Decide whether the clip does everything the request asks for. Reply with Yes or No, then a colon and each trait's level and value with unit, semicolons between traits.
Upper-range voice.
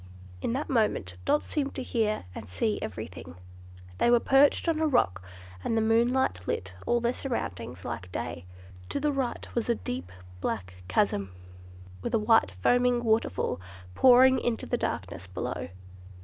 Yes: high, 225 Hz